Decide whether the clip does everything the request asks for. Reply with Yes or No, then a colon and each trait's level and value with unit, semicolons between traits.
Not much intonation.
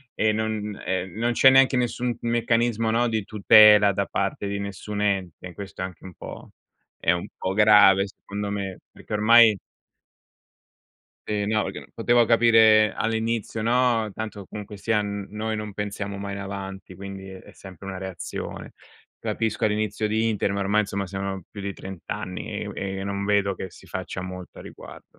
Yes: narrow, 2.1 semitones